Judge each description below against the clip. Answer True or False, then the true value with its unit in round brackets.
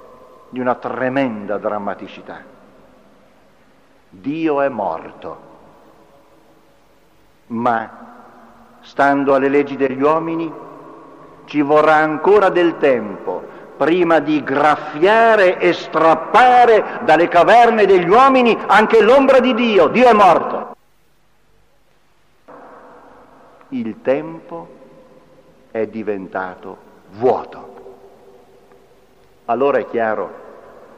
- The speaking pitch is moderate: True (160 Hz)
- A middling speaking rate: False (80 wpm)